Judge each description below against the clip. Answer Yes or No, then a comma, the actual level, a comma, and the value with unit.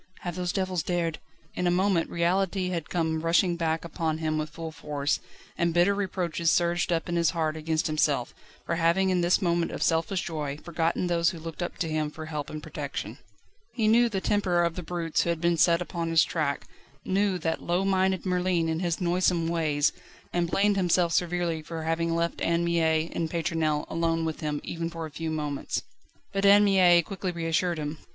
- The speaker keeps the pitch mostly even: Yes, narrow, 1.8 semitones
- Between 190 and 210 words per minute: Yes, fast, 205 wpm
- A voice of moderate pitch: Yes, medium, 170 Hz